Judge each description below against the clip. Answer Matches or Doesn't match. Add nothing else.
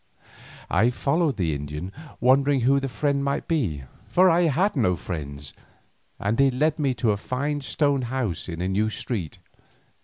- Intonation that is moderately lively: Doesn't match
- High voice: Doesn't match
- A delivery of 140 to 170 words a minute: Matches